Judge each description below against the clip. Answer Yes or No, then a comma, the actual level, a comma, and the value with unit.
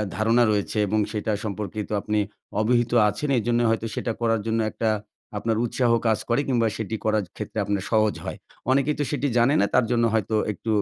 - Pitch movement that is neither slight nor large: No, narrow, 1.8 semitones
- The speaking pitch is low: Yes, low, 110 Hz